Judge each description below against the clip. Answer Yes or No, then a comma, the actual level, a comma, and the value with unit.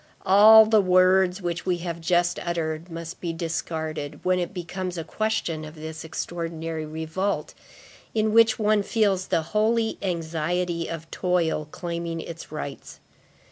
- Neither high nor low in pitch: Yes, medium, 175 Hz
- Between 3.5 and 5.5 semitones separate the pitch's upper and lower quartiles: No, average, 2.7 semitones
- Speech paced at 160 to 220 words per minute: No, average, 140 wpm